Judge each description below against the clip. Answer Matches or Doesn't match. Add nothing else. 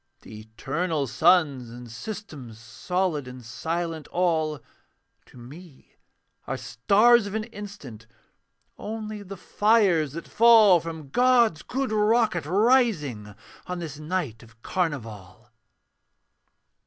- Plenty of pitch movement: Matches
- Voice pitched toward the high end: Doesn't match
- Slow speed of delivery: Matches